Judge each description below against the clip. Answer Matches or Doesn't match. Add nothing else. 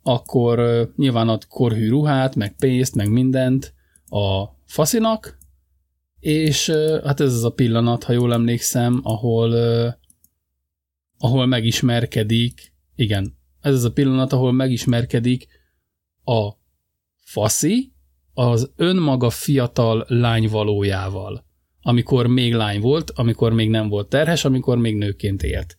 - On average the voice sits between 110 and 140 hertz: Matches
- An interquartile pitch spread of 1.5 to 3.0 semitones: Doesn't match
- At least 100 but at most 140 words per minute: Matches